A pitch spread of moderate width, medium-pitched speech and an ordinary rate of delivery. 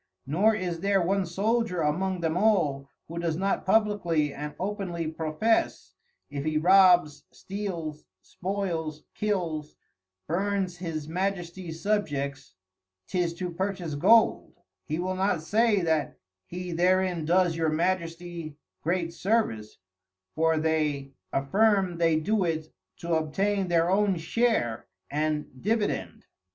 No: average, 3.7 semitones; medium, 175 Hz; slow, 120 wpm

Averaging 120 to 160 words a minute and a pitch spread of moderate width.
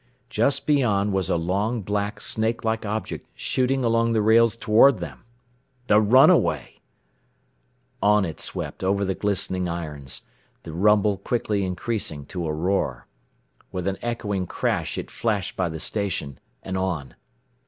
Yes: average, 145 wpm; average, 3.5 semitones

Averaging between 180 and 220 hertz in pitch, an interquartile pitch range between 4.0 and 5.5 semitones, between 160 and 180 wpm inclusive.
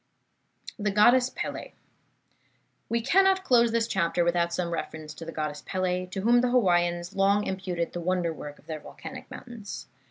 Yes: medium, 185 Hz; average, 5.2 semitones; average, 165 wpm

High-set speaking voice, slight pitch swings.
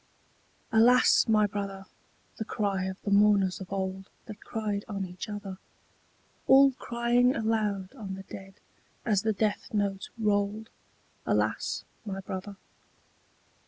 Yes: high, 205 Hz; narrow, 2.3 semitones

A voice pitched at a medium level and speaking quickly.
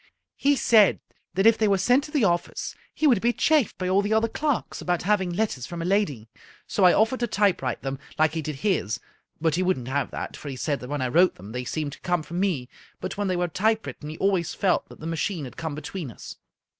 Yes: medium, 180 Hz; fast, 250 wpm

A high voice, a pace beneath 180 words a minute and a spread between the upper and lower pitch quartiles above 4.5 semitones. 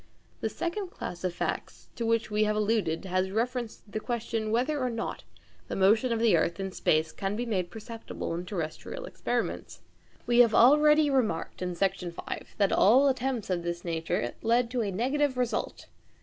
No: high, 220 Hz; average, 185 wpm; average, 5.0 semitones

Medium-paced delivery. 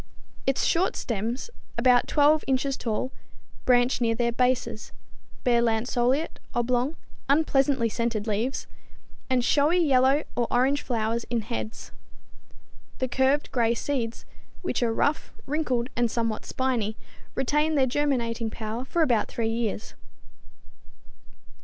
No: slow, 120 wpm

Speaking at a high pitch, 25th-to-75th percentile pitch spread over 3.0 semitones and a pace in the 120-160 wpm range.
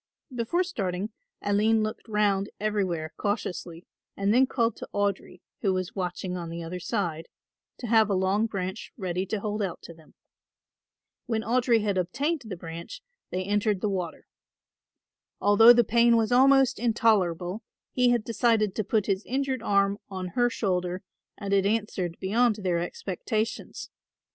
Yes: high, 205 Hz; average, 3.7 semitones; average, 155 wpm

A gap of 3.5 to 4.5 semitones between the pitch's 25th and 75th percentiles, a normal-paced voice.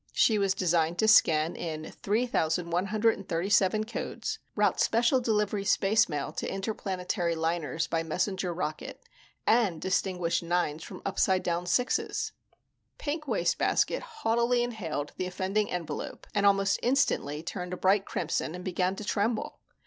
No: average, 4.0 semitones; slow, 130 wpm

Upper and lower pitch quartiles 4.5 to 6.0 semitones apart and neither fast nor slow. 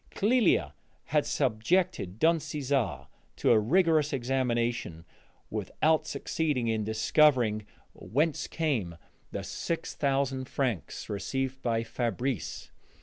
No: wide, 5.5 semitones; slow, 100 wpm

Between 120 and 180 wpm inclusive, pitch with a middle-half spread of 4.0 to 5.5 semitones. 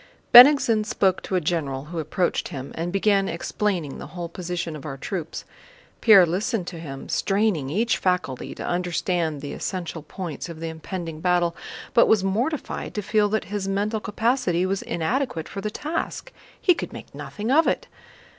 Yes: average, 175 wpm; average, 4.4 semitones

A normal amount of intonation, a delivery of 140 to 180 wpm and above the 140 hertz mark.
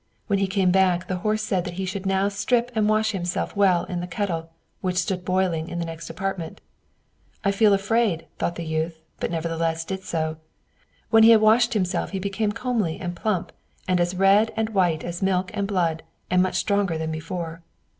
No: average, 3.0 semitones; average, 200 wpm; medium, 185 Hz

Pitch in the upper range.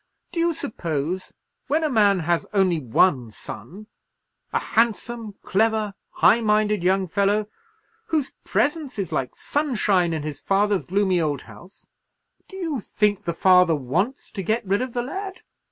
Yes: high, 205 Hz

